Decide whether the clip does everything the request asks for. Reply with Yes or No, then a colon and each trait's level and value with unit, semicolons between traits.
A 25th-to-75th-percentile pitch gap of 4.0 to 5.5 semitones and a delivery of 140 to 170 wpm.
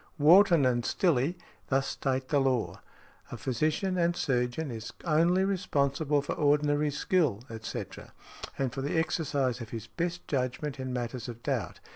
Yes: average, 4.3 semitones; average, 150 wpm